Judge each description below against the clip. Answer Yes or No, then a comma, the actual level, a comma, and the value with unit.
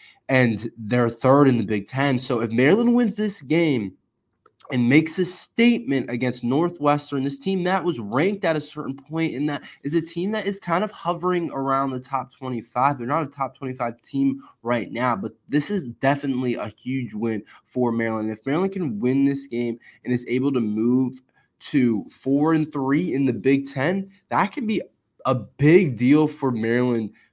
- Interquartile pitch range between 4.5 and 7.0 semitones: Yes, average, 5.1 semitones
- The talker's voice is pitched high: No, low, 135 Hz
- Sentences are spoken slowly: No, average, 190 wpm